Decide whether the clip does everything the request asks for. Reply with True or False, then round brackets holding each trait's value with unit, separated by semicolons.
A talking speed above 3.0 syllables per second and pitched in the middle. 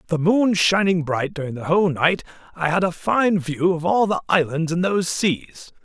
True (4.9 syllables/s; 175 Hz)